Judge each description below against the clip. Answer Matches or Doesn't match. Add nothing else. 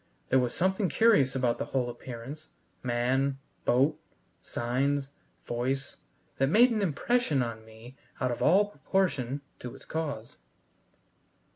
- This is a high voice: Doesn't match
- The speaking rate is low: Matches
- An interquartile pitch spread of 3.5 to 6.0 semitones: Matches